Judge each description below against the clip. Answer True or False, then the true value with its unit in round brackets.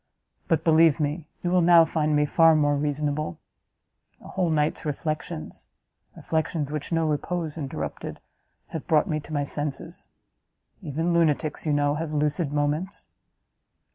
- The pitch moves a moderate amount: False (1.9 semitones)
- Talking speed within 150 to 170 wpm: False (140 wpm)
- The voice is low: False (155 Hz)